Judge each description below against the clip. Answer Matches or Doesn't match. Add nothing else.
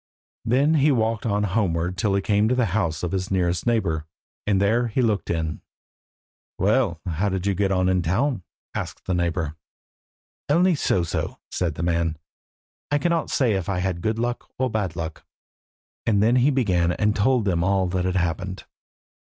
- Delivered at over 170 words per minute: Matches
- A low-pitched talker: Matches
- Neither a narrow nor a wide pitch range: Matches